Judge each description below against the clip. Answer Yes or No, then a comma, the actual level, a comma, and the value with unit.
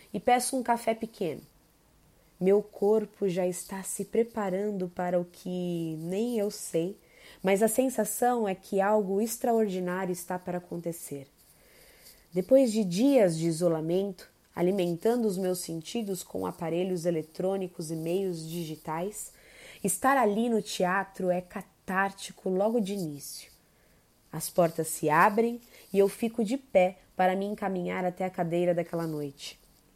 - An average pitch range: Yes, average, 3.3 semitones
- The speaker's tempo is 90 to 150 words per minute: Yes, average, 135 wpm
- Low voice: No, high, 190 Hz